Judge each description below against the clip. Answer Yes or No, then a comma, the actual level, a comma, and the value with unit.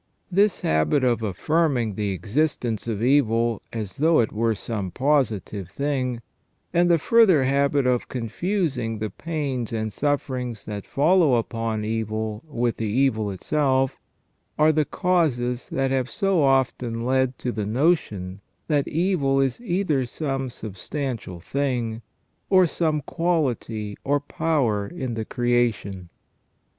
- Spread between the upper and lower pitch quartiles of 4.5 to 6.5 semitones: Yes, average, 5.0 semitones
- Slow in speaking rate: Yes, slow, 130 wpm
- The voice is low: Yes, low, 125 Hz